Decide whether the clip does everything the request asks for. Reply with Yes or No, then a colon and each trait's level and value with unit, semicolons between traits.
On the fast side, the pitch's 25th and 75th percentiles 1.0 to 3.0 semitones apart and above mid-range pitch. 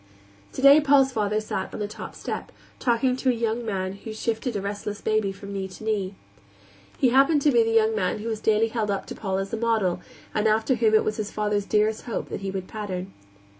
Yes: fast, 230 wpm; narrow, 2.4 semitones; high, 215 Hz